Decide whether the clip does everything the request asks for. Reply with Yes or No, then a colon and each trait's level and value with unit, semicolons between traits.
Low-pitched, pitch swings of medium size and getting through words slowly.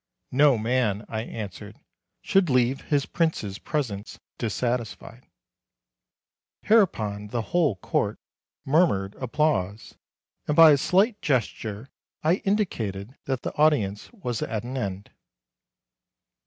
No: low, 125 Hz; wide, 6.5 semitones; slow, 110 wpm